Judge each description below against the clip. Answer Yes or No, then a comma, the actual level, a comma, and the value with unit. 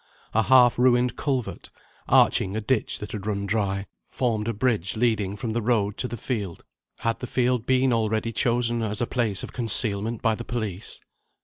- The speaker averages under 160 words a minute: No, average, 185 wpm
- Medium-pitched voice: No, low, 115 Hz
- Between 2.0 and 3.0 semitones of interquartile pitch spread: Yes, average, 2.7 semitones